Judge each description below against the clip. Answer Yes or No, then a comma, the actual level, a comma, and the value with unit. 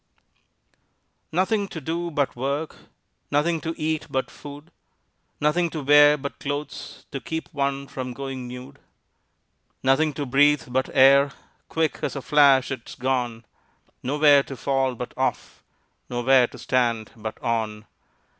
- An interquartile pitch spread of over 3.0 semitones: No, average, 2.7 semitones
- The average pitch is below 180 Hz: Yes, medium, 140 Hz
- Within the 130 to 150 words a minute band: Yes, slow, 135 wpm